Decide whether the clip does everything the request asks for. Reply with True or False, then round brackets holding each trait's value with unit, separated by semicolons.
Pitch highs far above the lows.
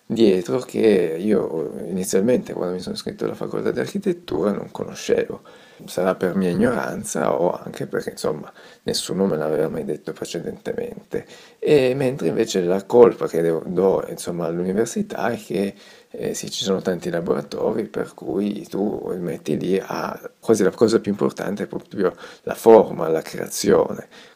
True (6.0 semitones)